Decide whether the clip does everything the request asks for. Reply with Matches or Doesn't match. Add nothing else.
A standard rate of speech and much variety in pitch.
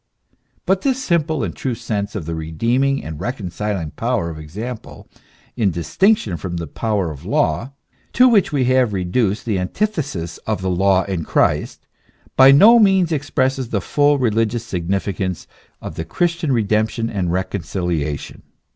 Matches